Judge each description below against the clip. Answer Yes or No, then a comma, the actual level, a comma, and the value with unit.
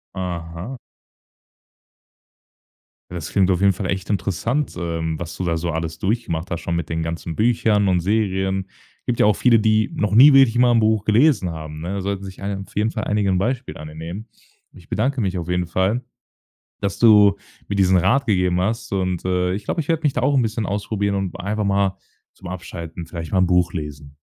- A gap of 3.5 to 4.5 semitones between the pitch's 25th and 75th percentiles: Yes, average, 3.9 semitones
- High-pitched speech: No, very low, 95 Hz